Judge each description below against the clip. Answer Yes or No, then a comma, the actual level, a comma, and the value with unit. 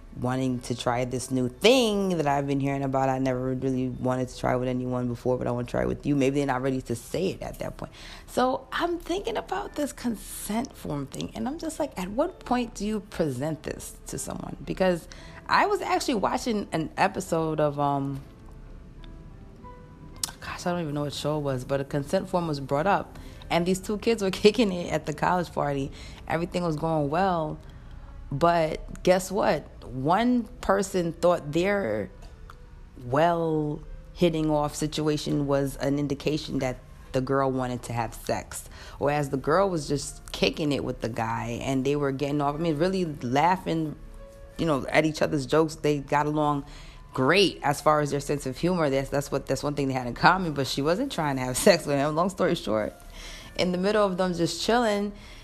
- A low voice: No, medium, 150 Hz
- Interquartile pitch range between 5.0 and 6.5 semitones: Yes, average, 5.3 semitones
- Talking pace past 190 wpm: Yes, average, 200 wpm